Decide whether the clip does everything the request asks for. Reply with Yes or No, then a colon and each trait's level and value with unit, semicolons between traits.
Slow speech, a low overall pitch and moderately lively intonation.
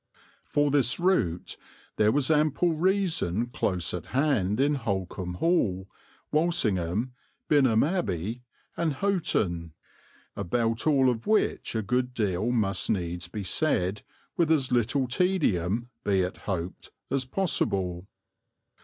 No: slow, 120 wpm; low, 120 Hz; wide, 7.9 semitones